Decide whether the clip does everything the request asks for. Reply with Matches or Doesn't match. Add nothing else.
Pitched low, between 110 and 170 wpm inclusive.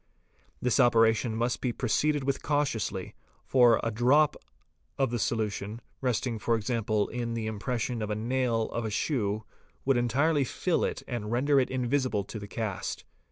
Matches